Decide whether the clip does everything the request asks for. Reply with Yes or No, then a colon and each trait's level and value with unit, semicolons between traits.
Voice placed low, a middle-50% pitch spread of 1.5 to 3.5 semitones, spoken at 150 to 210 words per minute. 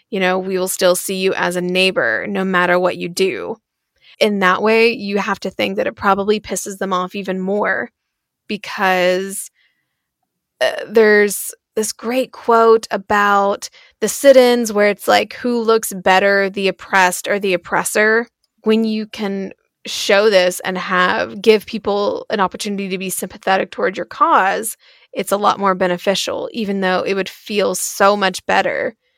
No: high, 200 Hz; average, 2.7 semitones; average, 165 wpm